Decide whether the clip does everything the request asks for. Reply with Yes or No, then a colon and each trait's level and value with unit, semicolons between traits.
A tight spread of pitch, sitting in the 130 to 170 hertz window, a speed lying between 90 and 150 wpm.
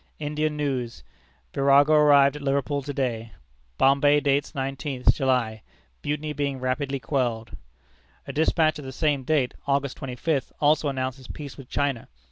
Yes: narrow, 2.0 semitones; medium, 140 Hz; average, 145 wpm